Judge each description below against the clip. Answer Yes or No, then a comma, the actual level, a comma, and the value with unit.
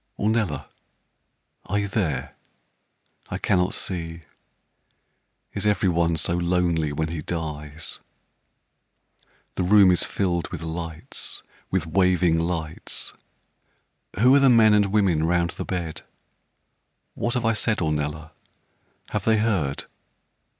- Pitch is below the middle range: Yes, very low, 85 Hz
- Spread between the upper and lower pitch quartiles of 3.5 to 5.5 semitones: Yes, average, 4.0 semitones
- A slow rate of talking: Yes, slow, 120 wpm